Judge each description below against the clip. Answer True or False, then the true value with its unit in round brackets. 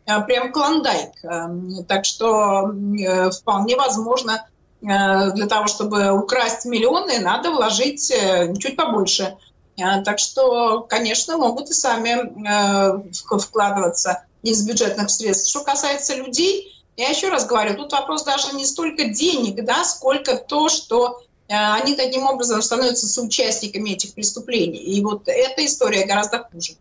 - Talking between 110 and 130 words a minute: True (125 wpm)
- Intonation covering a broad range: False (4.5 semitones)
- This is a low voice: False (220 Hz)